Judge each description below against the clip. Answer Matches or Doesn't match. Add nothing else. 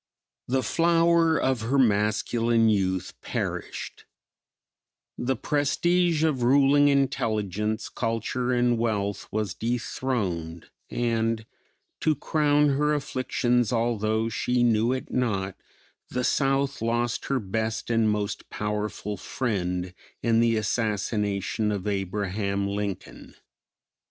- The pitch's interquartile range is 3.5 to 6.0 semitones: Matches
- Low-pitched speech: Matches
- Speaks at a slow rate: Matches